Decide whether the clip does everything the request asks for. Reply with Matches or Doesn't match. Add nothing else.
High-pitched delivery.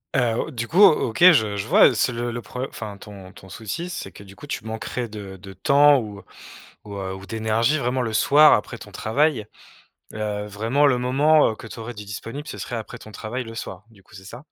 Doesn't match